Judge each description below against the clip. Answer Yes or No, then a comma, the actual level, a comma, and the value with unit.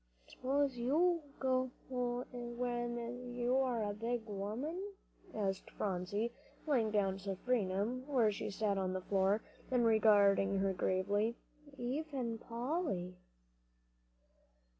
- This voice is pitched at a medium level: No, high, 230 Hz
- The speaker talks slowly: Yes, slow, 115 wpm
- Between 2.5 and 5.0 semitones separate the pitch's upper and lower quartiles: Yes, average, 3.9 semitones